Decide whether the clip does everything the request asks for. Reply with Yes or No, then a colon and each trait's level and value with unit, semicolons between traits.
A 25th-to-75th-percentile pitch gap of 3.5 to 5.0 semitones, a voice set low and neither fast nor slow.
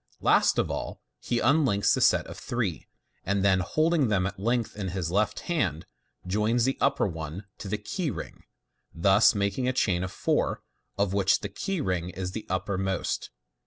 Yes: average, 4.2 semitones; low, 100 Hz; average, 180 wpm